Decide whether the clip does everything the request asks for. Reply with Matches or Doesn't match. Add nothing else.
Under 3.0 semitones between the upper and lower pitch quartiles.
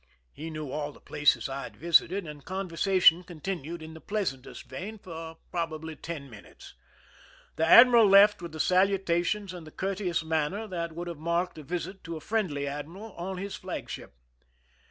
Doesn't match